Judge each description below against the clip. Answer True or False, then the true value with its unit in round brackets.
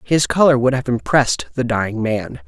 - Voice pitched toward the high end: False (120 Hz)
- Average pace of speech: True (195 wpm)